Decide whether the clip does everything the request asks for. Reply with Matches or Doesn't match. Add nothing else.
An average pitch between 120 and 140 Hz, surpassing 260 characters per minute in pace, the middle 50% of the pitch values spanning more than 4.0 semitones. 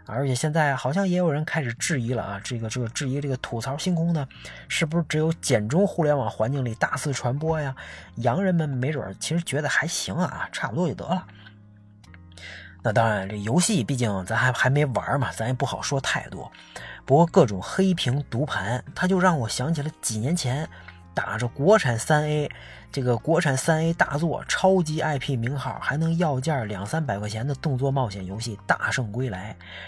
Matches